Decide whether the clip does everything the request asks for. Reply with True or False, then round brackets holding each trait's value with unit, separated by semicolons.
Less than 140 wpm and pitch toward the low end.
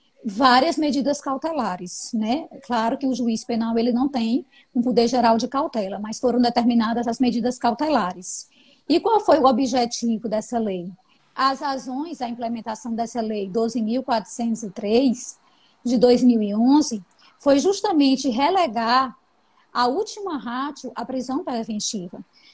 False (130 wpm; 245 Hz)